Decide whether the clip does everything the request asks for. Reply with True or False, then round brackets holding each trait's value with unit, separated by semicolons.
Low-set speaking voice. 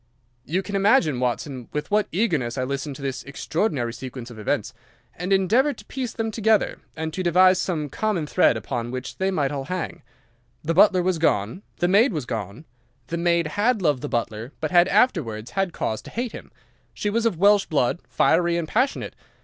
False (170 Hz)